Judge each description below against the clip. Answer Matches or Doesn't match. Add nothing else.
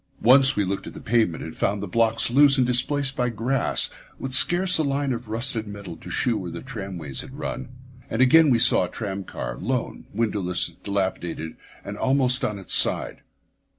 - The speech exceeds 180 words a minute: Matches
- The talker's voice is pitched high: Doesn't match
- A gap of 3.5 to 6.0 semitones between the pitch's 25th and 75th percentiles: Matches